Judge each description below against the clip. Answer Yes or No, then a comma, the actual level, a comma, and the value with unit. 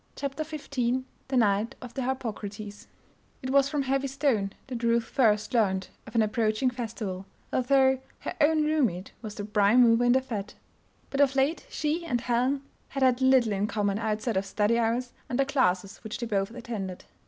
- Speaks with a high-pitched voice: Yes, high, 235 Hz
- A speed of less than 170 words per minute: No, average, 190 wpm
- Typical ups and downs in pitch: Yes, average, 4.1 semitones